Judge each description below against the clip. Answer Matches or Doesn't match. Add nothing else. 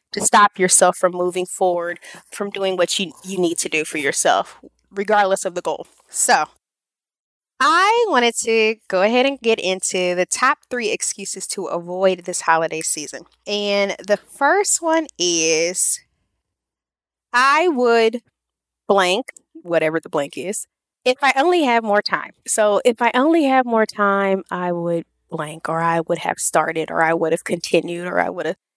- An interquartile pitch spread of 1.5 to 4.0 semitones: Doesn't match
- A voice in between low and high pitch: Doesn't match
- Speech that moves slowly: Doesn't match